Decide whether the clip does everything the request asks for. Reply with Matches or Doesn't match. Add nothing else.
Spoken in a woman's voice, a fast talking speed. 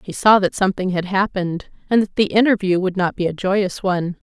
Matches